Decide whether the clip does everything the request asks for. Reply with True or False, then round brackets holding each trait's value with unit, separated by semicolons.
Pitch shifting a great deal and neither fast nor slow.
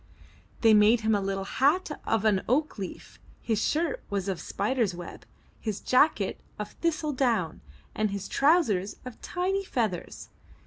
True (6.2 semitones; 145 wpm)